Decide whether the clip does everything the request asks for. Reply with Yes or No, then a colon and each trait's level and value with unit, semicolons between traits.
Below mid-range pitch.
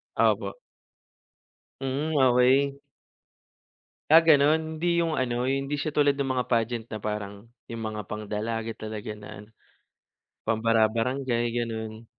Yes: low, 120 Hz